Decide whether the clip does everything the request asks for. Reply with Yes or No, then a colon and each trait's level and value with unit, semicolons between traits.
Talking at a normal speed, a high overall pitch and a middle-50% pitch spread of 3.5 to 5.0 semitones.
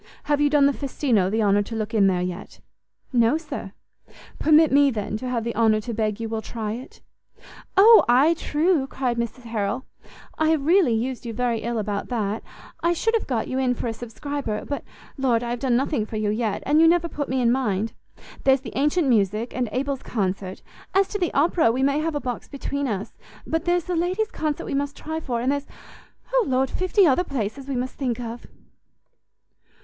No: fast, 210 wpm; very high, 255 Hz; average, 4.6 semitones